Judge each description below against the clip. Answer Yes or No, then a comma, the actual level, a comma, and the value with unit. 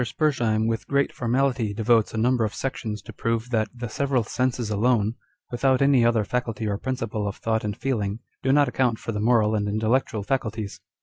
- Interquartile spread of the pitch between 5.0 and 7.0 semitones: No, average, 2.8 semitones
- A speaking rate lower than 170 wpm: No, average, 190 wpm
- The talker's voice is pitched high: No, low, 115 Hz